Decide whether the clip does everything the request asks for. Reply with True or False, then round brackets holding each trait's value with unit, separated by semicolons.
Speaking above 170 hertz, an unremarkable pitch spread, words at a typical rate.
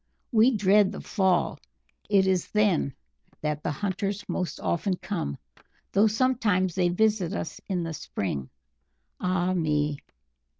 False (185 Hz; 3.9 semitones; 130 wpm)